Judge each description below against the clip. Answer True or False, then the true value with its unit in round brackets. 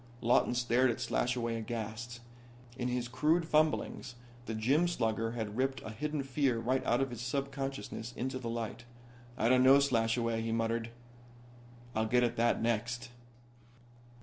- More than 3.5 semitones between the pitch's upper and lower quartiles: False (2.5 semitones)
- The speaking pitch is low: True (120 Hz)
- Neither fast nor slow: True (150 wpm)